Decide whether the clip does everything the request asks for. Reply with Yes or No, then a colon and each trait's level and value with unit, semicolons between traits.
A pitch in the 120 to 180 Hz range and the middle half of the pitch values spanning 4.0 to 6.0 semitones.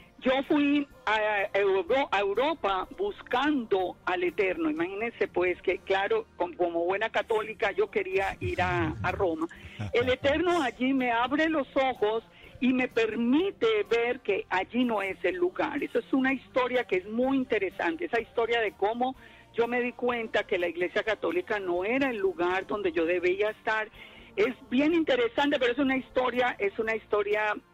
No: high, 240 Hz; average, 5.2 semitones